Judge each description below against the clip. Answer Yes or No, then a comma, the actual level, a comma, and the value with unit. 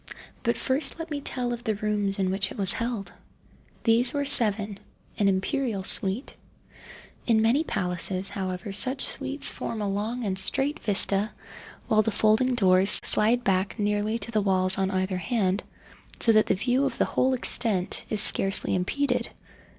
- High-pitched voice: Yes, high, 215 Hz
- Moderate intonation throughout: Yes, average, 4.0 semitones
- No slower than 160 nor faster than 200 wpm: Yes, average, 165 wpm